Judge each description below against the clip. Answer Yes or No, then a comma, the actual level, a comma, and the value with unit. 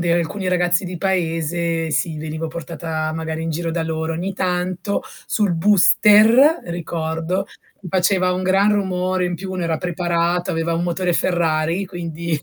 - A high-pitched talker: No, medium, 175 Hz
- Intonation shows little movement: Yes, narrow, 2.1 semitones